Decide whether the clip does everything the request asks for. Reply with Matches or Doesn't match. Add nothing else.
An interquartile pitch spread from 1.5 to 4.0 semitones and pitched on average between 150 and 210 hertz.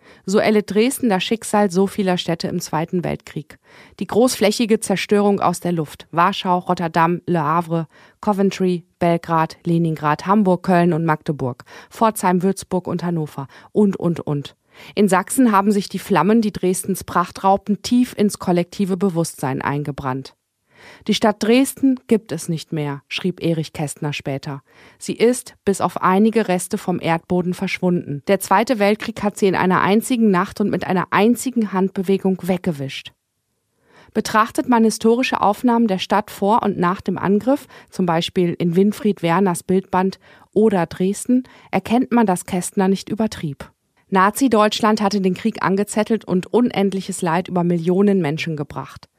Matches